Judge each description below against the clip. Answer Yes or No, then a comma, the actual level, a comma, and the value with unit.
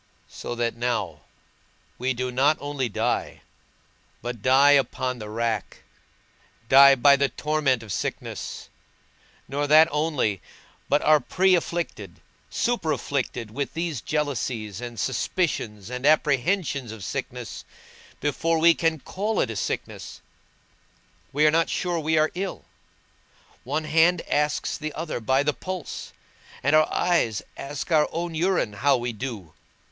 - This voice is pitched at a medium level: Yes, medium, 145 Hz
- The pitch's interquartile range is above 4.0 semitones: Yes, average, 4.7 semitones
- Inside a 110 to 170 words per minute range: Yes, average, 140 wpm